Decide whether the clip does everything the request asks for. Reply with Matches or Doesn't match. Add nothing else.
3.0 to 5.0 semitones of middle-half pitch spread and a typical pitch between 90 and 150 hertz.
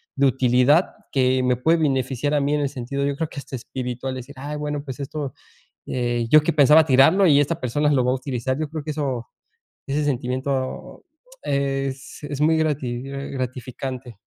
Doesn't match